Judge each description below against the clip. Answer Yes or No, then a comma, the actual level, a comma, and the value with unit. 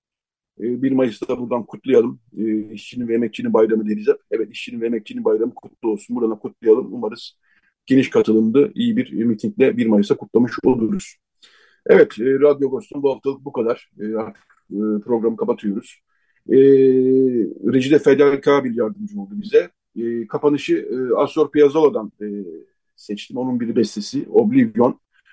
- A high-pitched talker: No, low, 135 Hz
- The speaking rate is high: No, average, 130 wpm